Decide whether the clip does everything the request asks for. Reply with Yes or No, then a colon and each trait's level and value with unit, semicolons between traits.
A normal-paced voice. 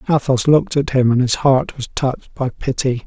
No: fast, 215 wpm